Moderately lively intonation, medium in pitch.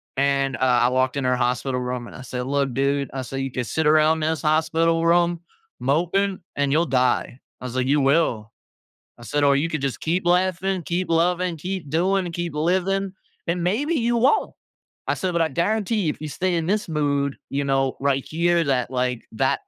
Yes: average, 4.5 semitones; medium, 155 Hz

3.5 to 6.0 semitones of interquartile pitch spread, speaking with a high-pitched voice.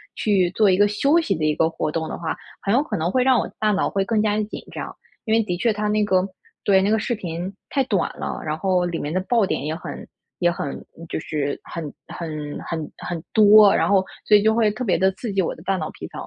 Yes: average, 4.1 semitones; high, 195 Hz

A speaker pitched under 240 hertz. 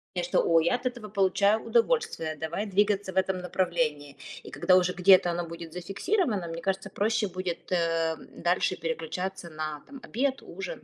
Yes: medium, 185 Hz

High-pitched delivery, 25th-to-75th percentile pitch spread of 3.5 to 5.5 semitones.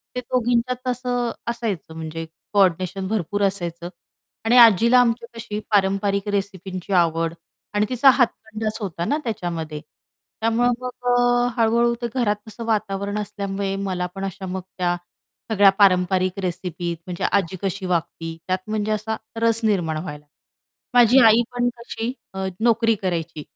Yes: high, 205 Hz; average, 4.1 semitones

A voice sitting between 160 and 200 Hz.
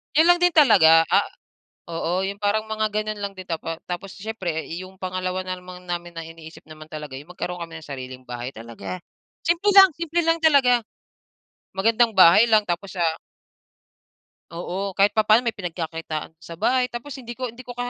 Yes: medium, 185 Hz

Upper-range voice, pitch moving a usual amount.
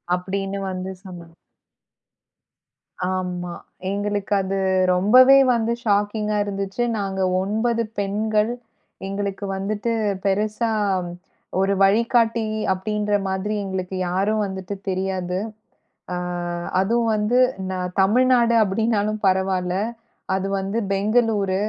No: high, 200 Hz; narrow, 2.3 semitones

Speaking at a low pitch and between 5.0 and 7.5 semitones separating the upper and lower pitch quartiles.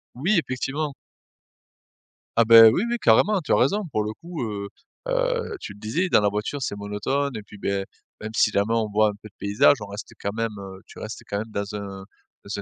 Yes: low, 110 Hz; wide, 5.6 semitones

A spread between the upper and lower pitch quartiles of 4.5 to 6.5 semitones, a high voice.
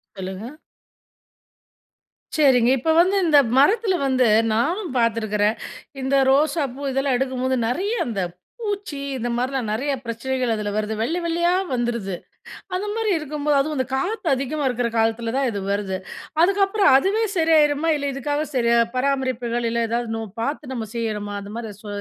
Yes: average, 4.9 semitones; very high, 260 Hz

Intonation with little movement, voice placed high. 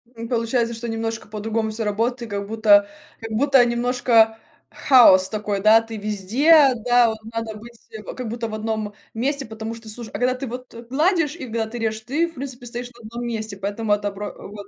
Yes: narrow, 2.2 semitones; high, 225 Hz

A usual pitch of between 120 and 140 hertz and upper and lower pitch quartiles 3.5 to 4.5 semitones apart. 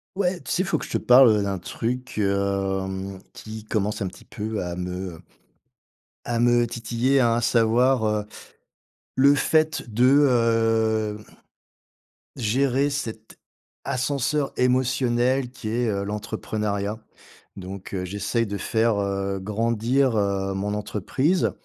No: low, 110 Hz; average, 3.9 semitones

